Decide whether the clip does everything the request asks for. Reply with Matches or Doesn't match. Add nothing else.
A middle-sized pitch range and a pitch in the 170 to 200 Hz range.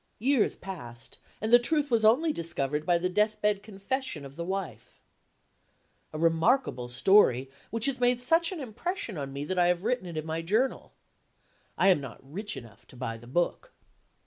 Doesn't match